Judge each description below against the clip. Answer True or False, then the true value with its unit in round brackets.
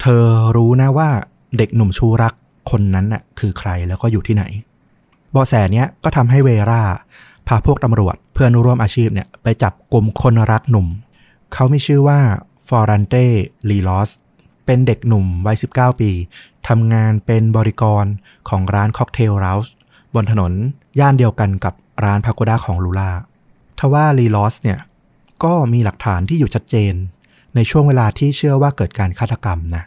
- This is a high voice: False (115 Hz)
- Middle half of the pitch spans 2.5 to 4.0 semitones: True (3.6 semitones)